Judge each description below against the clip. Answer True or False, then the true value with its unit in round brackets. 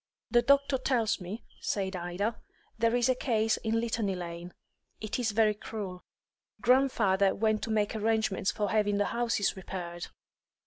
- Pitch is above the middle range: True (215 Hz)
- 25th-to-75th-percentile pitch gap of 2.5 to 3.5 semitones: True (3.1 semitones)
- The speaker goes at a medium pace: True (150 wpm)